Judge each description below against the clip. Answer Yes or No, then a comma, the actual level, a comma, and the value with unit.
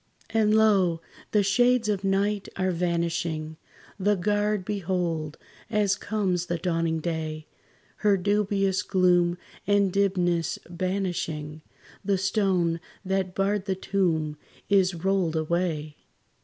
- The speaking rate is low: Yes, slow, 115 wpm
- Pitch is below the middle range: No, medium, 185 Hz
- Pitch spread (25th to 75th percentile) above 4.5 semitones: No, average, 3.0 semitones